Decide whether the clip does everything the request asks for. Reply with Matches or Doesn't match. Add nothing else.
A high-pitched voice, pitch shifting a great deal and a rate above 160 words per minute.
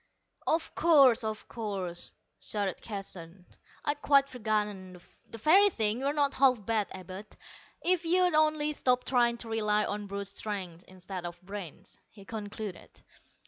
Doesn't match